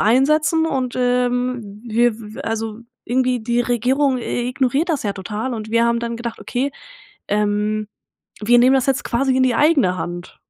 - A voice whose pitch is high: Yes, high, 240 Hz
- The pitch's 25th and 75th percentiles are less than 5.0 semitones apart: Yes, average, 2.9 semitones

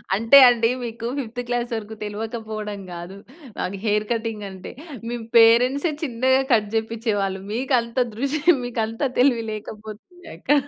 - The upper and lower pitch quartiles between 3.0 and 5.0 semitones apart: No, narrow, 2.6 semitones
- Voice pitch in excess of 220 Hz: Yes, high, 230 Hz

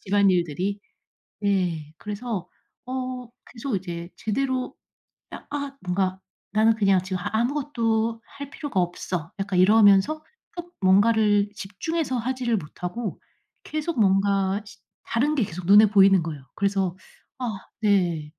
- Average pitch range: Yes, average, 4.3 semitones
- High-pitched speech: Yes, high, 205 Hz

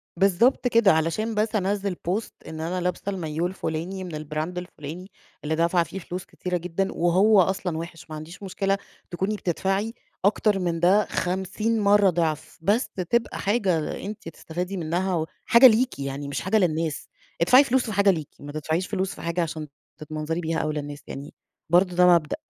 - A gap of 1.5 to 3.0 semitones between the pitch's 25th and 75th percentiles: No, average, 3.7 semitones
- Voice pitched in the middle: Yes, medium, 180 Hz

